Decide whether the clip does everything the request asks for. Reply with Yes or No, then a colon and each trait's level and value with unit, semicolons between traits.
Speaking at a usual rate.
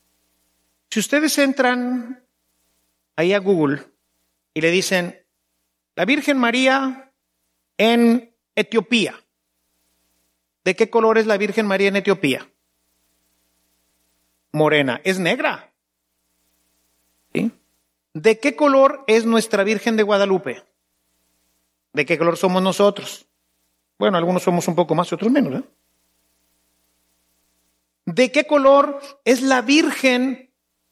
No: slow, 105 wpm